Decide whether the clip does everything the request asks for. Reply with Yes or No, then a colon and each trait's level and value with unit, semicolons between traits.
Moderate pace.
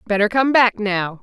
Yes: average, 195 wpm